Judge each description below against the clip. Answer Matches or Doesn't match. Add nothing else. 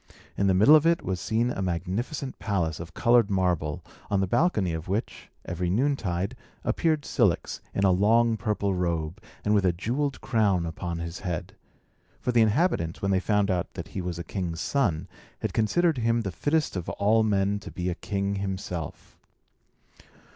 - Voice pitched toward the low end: Matches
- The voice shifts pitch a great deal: Doesn't match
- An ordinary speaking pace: Matches